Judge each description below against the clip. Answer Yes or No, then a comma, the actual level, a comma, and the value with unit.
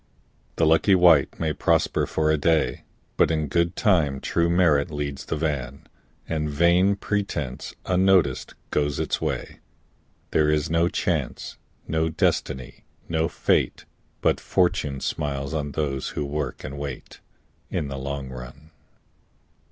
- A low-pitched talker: Yes, very low, 75 Hz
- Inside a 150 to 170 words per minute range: No, slow, 135 wpm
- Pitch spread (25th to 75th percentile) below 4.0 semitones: Yes, average, 2.9 semitones